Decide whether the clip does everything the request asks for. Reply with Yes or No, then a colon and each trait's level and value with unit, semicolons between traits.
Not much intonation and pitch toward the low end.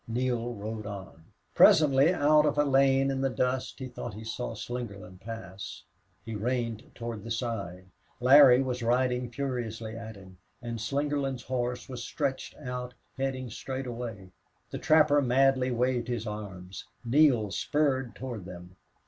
No: average, 3.2 semitones; low, 125 Hz